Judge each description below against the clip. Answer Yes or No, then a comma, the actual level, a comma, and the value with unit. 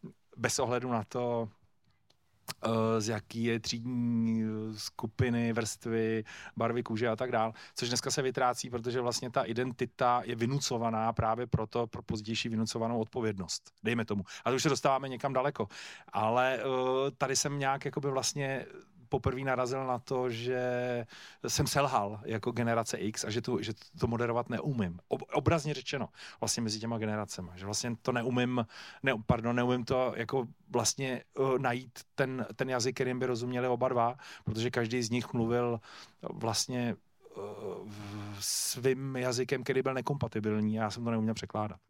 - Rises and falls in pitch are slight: Yes, narrow, 2.3 semitones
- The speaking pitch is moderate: No, low, 120 Hz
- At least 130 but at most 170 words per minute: Yes, average, 150 wpm